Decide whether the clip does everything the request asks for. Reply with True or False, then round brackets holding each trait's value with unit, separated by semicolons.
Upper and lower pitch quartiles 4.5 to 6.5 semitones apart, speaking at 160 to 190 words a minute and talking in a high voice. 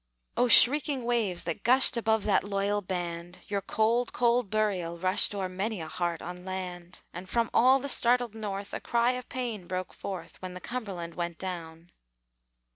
True (4.8 semitones; 175 wpm; 200 Hz)